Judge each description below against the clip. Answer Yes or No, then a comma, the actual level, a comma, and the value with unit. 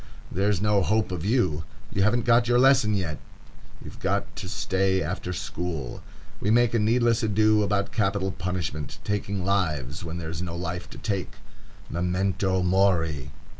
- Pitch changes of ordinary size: Yes, average, 3.3 semitones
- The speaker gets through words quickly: No, average, 155 wpm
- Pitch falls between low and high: No, very low, 95 Hz